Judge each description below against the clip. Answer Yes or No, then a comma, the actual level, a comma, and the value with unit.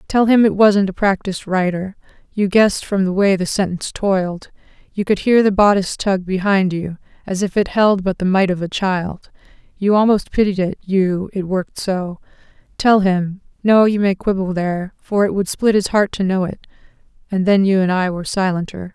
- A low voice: No, high, 190 Hz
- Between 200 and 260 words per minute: Yes, fast, 205 wpm